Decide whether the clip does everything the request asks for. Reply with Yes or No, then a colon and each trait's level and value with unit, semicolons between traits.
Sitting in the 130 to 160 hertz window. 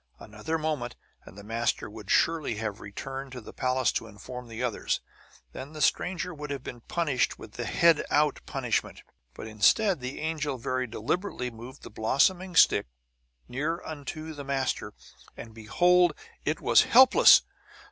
Yes: low, 135 Hz